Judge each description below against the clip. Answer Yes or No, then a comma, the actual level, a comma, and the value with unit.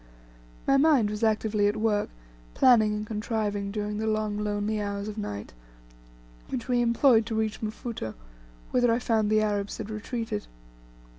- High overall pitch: Yes, high, 215 Hz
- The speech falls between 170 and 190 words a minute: No, average, 155 wpm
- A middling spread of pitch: No, narrow, 1.5 semitones